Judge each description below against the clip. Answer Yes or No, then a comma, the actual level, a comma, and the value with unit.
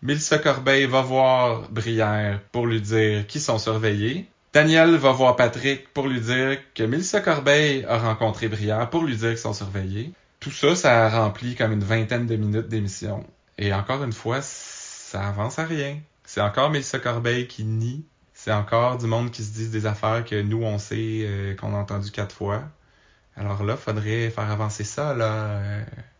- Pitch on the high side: No, low, 115 Hz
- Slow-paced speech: No, average, 190 wpm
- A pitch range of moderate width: Yes, average, 3.8 semitones